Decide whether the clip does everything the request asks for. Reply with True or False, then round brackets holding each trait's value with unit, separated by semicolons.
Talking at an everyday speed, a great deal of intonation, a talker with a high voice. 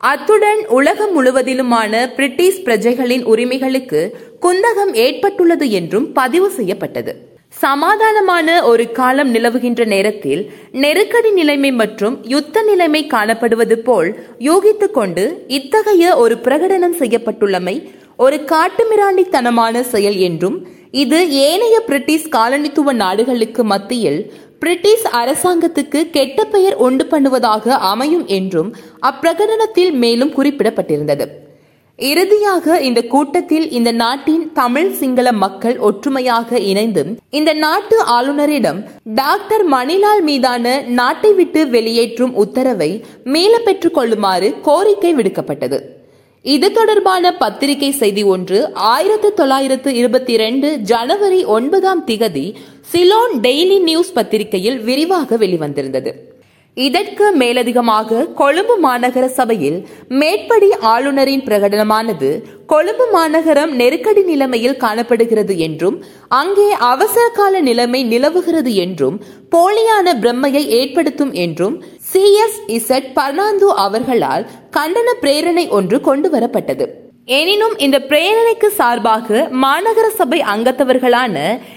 True (95 wpm; 7.3 semitones; 275 Hz)